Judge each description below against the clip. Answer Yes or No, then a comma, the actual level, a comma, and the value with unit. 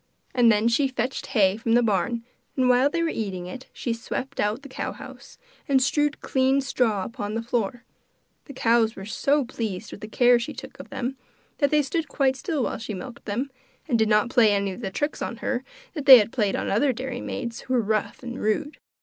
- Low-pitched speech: No, high, 240 Hz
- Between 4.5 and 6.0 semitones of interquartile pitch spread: No, average, 3.6 semitones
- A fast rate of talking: Yes, fast, 220 wpm